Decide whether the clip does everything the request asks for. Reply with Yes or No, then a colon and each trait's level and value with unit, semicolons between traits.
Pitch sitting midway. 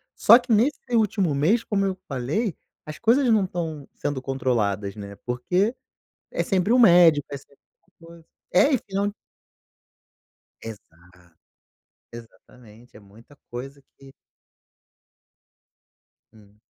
Yes: medium, 145 Hz